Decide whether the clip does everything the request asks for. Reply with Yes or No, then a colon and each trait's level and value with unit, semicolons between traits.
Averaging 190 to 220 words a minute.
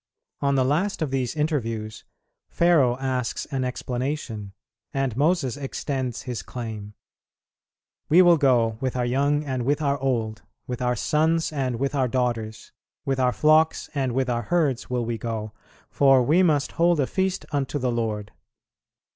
No: average, 160 wpm